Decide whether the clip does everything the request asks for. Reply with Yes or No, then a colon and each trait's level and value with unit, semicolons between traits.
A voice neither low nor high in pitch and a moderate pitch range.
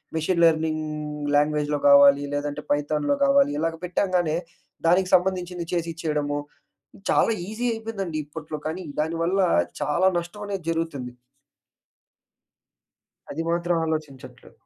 Yes: medium, 160 Hz; average, 3.4 semitones